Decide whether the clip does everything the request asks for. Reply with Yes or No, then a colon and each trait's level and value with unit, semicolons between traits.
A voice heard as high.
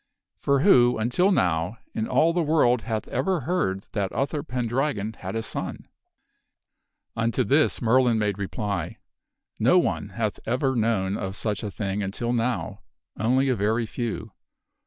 No: low, 115 Hz